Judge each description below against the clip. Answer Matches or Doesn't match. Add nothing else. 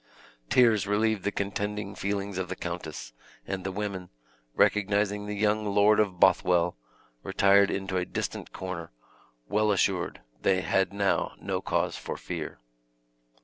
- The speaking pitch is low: Matches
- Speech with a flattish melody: Matches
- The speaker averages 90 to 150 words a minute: Matches